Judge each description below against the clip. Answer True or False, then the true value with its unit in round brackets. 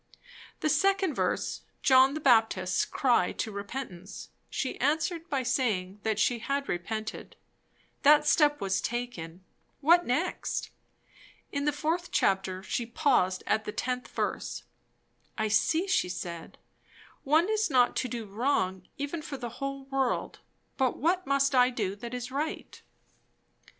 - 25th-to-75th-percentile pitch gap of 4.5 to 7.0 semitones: True (5.3 semitones)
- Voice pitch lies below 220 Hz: False (255 Hz)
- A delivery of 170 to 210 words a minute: False (140 wpm)